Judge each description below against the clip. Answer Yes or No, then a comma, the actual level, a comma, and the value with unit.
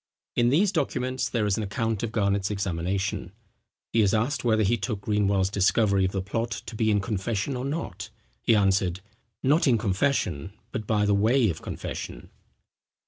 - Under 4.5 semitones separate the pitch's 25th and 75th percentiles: Yes, average, 3.2 semitones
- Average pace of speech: Yes, average, 170 wpm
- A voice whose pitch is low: Yes, low, 105 Hz